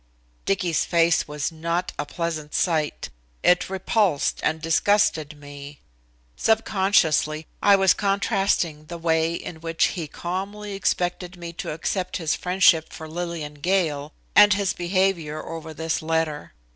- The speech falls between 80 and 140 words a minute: Yes, slow, 135 wpm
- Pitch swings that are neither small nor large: Yes, average, 3.3 semitones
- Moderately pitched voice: Yes, medium, 170 Hz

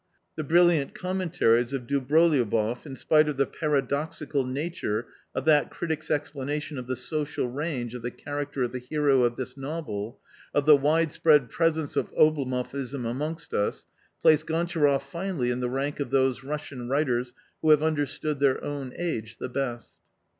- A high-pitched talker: No, medium, 140 Hz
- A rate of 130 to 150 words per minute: No, average, 165 wpm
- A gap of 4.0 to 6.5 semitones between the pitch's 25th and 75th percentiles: No, average, 3.5 semitones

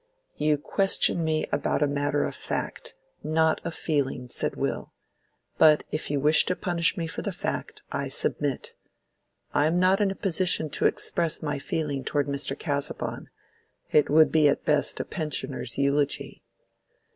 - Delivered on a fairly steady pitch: Yes, narrow, 2.3 semitones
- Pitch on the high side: No, medium, 150 Hz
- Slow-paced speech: No, average, 160 wpm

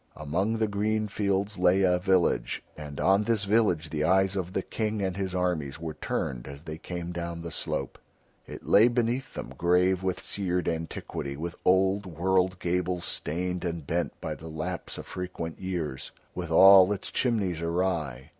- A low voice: Yes, very low, 90 Hz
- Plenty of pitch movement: No, average, 2.8 semitones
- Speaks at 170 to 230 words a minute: Yes, average, 175 wpm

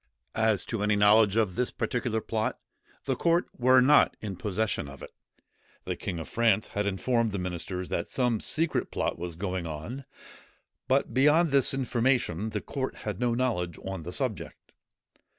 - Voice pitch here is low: Yes, low, 110 Hz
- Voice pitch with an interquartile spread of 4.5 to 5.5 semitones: Yes, average, 5.2 semitones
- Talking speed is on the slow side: No, average, 170 wpm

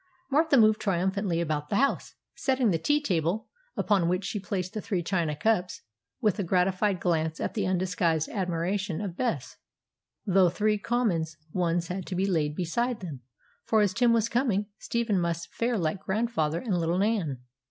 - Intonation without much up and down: No, average, 4.2 semitones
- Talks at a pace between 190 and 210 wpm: No, average, 175 wpm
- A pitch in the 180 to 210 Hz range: Yes, high, 190 Hz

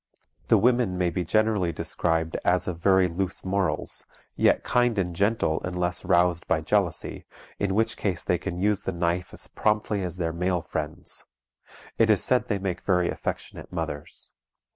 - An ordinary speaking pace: Yes, average, 165 wpm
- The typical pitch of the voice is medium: No, very low, 90 Hz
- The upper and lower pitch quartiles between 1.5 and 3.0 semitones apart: Yes, average, 2.7 semitones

